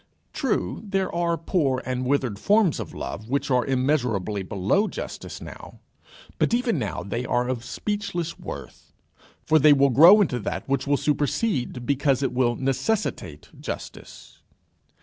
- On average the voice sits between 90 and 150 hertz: Yes, medium, 140 Hz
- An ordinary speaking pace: Yes, average, 150 wpm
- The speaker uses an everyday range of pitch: No, wide, 5.7 semitones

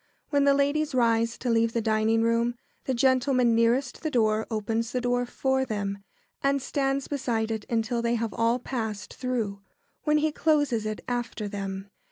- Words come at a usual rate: Yes, average, 180 wpm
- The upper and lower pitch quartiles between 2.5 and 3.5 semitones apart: Yes, average, 3.1 semitones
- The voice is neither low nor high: No, high, 235 Hz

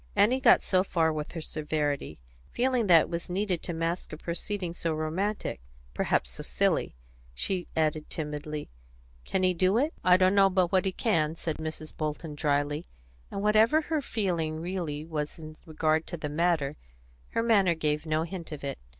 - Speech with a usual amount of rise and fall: Yes, average, 3.7 semitones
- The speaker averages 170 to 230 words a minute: Yes, average, 175 wpm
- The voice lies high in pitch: No, medium, 165 Hz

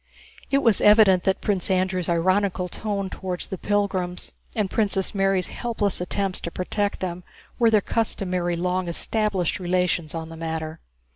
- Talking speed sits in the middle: Yes, average, 150 wpm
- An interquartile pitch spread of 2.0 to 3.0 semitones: Yes, narrow, 2.4 semitones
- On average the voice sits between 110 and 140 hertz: No, medium, 185 Hz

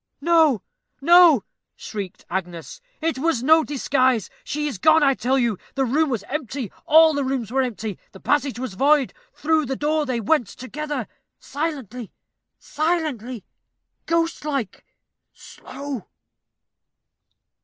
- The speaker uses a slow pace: Yes, slow, 125 wpm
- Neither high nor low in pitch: No, very high, 275 Hz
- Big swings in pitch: No, average, 4.4 semitones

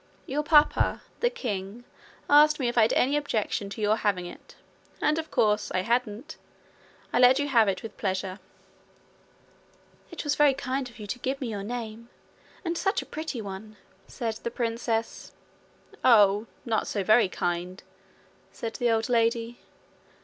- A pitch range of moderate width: Yes, average, 4.1 semitones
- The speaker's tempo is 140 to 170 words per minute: Yes, average, 165 wpm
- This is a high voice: Yes, high, 230 Hz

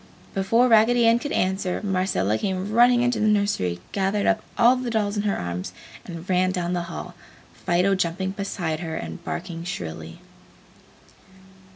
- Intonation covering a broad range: No, average, 3.9 semitones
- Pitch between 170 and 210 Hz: Yes, high, 190 Hz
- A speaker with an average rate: Yes, average, 160 wpm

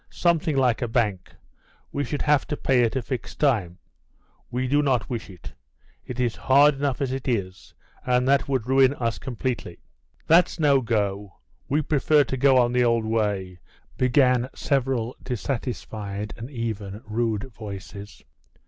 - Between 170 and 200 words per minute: No, average, 155 wpm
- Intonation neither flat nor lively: Yes, average, 3.7 semitones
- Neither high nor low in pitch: No, low, 125 Hz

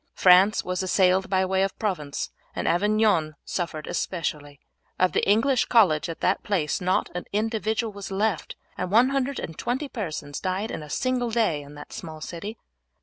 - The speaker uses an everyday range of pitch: Yes, average, 4.9 semitones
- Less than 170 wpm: Yes, average, 160 wpm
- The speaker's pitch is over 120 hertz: Yes, high, 190 Hz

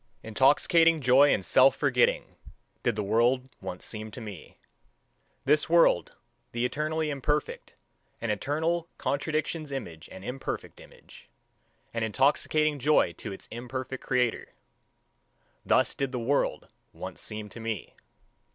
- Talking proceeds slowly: Yes, slow, 125 wpm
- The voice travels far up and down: No, average, 4.7 semitones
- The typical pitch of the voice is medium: No, low, 130 Hz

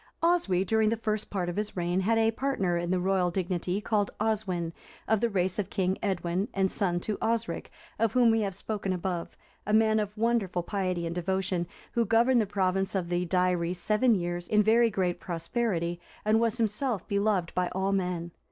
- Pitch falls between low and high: No, high, 195 Hz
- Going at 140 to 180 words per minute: No, average, 195 wpm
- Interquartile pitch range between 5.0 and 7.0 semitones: No, average, 3.5 semitones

